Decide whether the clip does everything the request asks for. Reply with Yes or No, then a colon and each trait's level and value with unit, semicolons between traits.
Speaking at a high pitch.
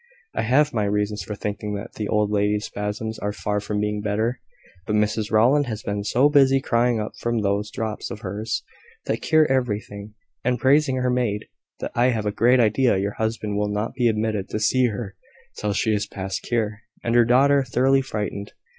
No: low, 110 Hz